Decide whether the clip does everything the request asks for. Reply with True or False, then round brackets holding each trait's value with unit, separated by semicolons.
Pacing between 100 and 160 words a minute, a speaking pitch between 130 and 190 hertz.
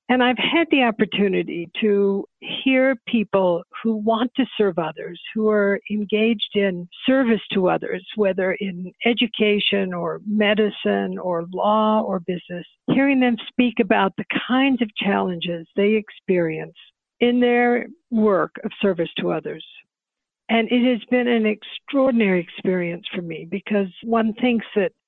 False (140 wpm; 215 Hz)